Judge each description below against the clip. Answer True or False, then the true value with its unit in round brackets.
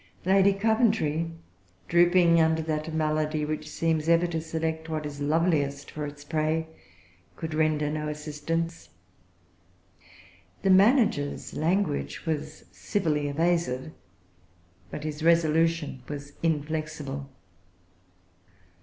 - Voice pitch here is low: False (155 Hz)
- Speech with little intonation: True (1.9 semitones)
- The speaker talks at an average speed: False (100 wpm)